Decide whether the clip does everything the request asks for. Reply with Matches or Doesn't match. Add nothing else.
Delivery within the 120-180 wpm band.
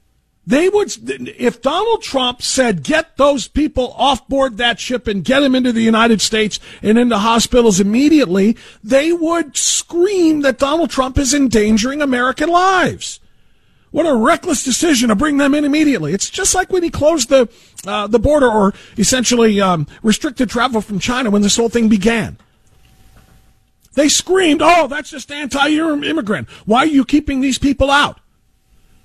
Matches